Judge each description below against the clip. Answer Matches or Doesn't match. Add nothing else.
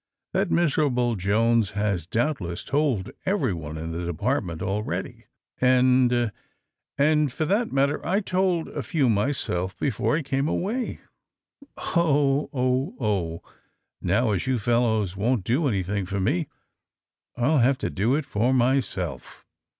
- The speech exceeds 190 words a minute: Doesn't match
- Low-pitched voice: Matches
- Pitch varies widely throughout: Matches